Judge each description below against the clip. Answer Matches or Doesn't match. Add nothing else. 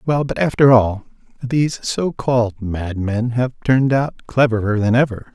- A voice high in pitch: Doesn't match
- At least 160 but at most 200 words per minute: Doesn't match